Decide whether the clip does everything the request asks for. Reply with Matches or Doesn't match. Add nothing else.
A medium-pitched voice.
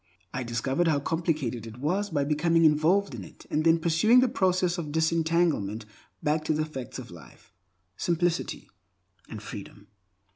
Matches